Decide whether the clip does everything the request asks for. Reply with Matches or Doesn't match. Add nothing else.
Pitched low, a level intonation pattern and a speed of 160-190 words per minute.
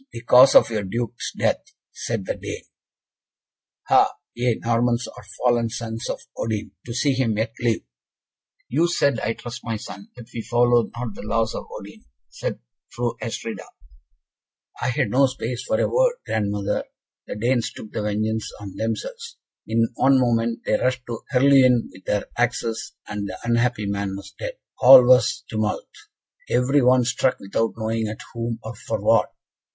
Matches